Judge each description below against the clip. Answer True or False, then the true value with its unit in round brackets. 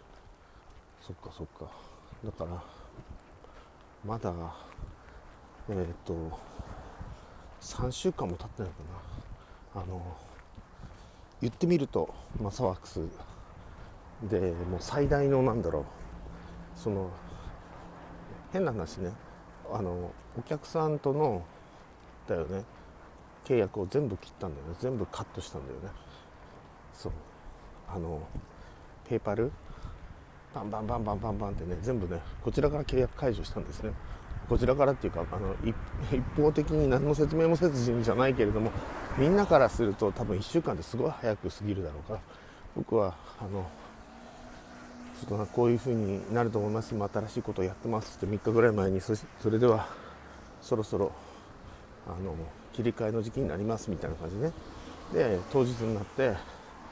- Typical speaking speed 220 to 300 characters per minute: True (285 characters per minute)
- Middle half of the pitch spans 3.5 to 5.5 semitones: True (5.2 semitones)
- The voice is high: False (100 Hz)